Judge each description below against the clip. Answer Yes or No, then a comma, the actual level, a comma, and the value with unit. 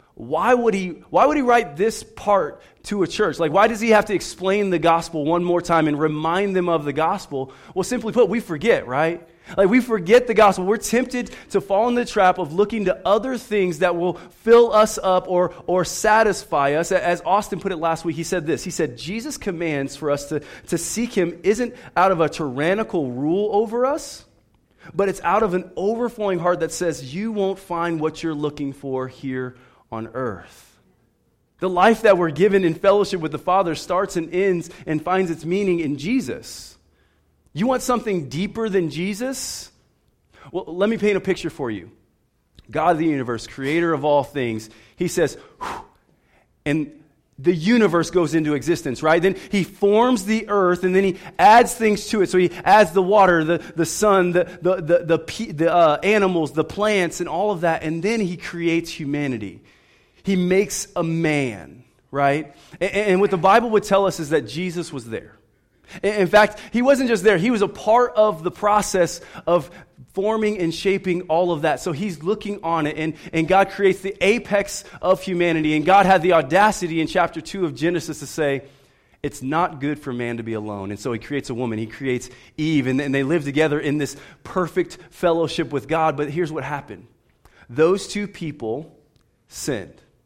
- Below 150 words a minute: No, average, 195 wpm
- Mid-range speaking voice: Yes, medium, 175 Hz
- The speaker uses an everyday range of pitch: Yes, average, 4.5 semitones